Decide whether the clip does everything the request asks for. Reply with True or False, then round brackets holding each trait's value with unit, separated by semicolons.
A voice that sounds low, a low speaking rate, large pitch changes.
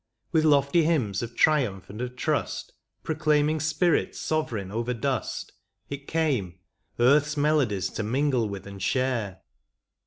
True (130 Hz; 130 wpm; 5.9 semitones)